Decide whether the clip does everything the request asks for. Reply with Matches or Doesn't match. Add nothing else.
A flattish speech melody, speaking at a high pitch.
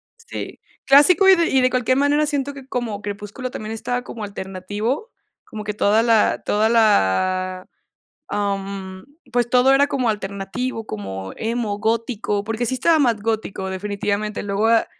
Doesn't match